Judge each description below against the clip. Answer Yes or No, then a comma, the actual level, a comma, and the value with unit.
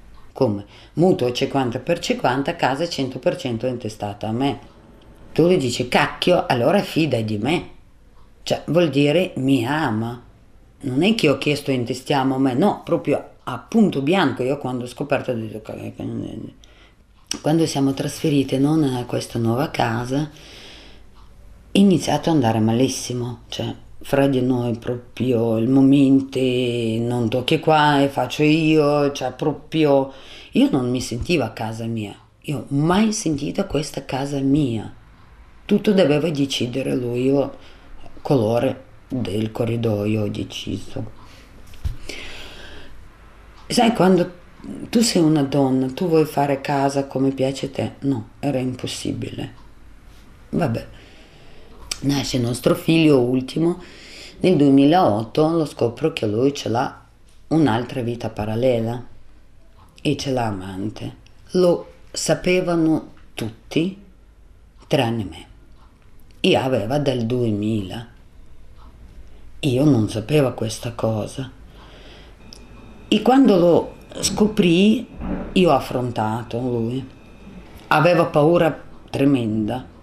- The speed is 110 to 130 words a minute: Yes, average, 120 wpm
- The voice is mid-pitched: No, low, 130 Hz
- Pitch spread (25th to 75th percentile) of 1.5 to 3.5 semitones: No, average, 4.8 semitones